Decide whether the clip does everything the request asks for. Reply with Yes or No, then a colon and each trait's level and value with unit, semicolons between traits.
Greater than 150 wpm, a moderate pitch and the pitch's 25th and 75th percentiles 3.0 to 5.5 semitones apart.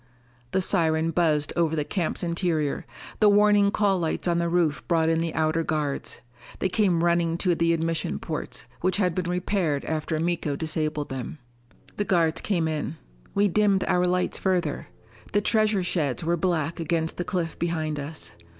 No: average, 170 wpm; medium, 170 Hz; narrow, 2.4 semitones